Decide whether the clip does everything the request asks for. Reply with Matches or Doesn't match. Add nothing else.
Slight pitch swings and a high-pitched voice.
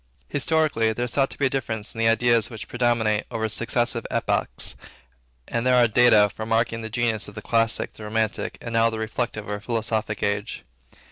Doesn't match